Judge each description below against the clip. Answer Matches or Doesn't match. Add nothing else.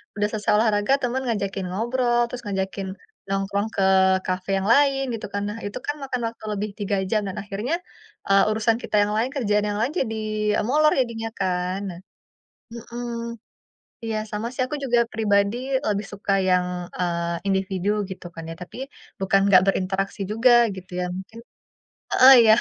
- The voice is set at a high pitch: Matches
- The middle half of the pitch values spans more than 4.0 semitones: Doesn't match